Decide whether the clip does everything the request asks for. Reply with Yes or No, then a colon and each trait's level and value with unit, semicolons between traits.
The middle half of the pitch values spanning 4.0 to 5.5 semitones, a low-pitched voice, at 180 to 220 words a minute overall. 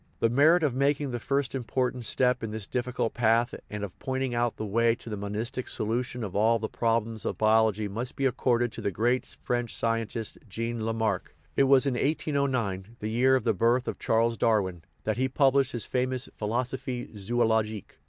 No: narrow, 2.6 semitones; low, 120 Hz; average, 190 wpm